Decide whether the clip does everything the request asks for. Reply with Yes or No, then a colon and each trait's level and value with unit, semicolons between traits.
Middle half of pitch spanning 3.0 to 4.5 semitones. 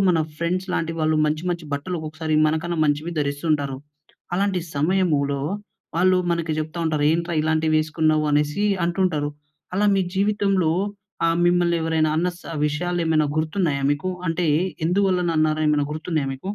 No: narrow, 2.5 semitones